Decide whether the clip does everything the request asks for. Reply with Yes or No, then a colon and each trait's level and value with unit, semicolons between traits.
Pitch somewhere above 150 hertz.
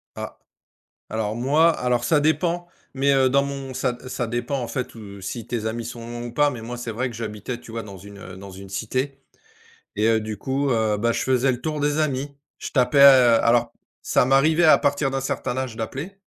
No: low, 125 Hz